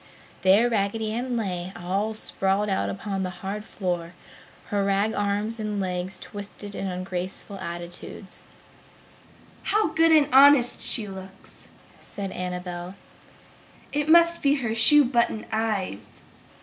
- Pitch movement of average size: Yes, average, 3.5 semitones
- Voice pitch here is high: Yes, high, 205 Hz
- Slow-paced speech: Yes, slow, 125 wpm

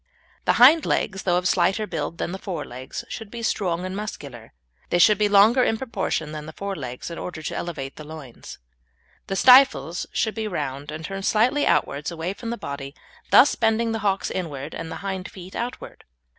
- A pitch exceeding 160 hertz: Yes, medium, 185 Hz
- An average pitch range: No, wide, 5.7 semitones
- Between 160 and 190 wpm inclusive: No, average, 200 wpm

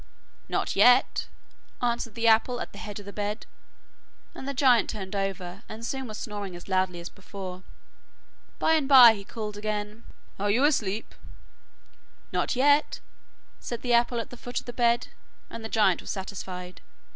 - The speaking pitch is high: Yes, high, 215 Hz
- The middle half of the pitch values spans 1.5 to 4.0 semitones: Yes, average, 3.5 semitones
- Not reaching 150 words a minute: No, average, 170 wpm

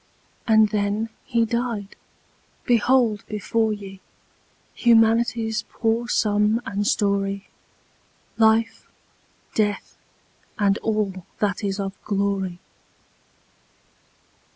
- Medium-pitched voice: No, high, 215 Hz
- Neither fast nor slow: No, slow, 80 wpm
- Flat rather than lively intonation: Yes, narrow, 2.1 semitones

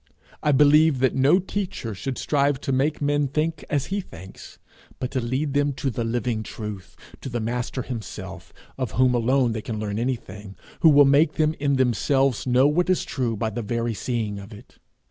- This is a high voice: No, low, 130 Hz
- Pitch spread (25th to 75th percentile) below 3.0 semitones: No, average, 4.1 semitones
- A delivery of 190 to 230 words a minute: Yes, average, 195 wpm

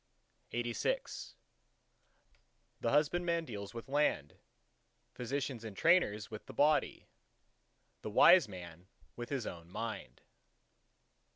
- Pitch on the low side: Yes, low, 120 Hz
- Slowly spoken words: Yes, slow, 100 wpm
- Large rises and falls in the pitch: Yes, wide, 6.4 semitones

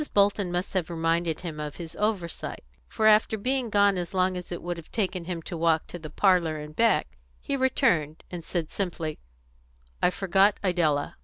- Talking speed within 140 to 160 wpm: No, average, 185 wpm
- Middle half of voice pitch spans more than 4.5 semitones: No, average, 3.6 semitones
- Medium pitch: Yes, medium, 175 Hz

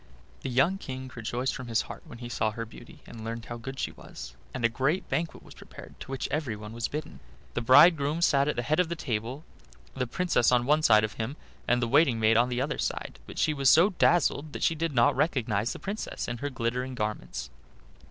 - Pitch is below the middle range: Yes, low, 130 Hz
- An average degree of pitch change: Yes, average, 4.5 semitones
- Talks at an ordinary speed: No, fast, 225 wpm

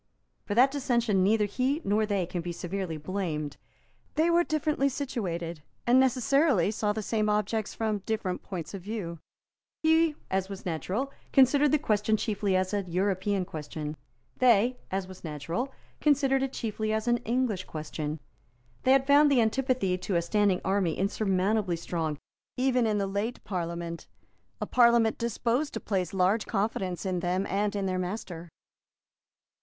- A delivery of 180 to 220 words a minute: No, average, 160 wpm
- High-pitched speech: Yes, high, 205 Hz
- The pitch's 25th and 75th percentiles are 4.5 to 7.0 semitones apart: Yes, average, 4.9 semitones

